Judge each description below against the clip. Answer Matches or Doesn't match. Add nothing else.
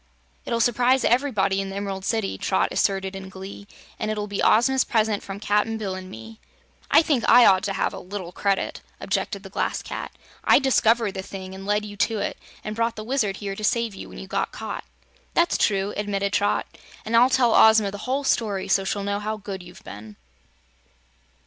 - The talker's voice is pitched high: Matches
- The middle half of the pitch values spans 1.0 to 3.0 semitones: Matches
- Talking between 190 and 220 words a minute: Matches